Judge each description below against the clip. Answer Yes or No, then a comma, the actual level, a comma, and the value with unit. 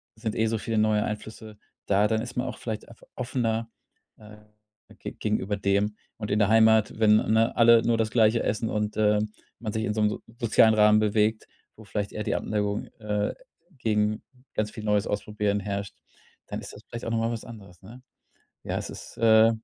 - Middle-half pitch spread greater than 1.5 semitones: No, narrow, 1.2 semitones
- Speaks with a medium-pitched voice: No, low, 110 Hz